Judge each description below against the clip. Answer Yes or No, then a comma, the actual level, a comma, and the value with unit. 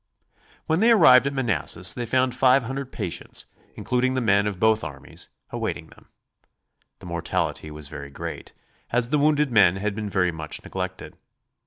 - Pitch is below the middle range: Yes, low, 115 Hz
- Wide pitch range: Yes, wide, 5.7 semitones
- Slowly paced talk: No, average, 165 wpm